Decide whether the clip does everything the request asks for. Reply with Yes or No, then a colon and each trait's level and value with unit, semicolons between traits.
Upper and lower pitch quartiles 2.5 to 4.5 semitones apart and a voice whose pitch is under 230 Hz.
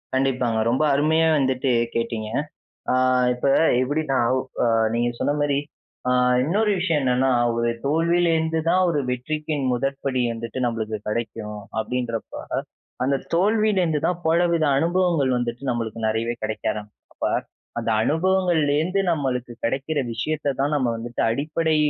No: average, 5.3 semitones; medium, 140 Hz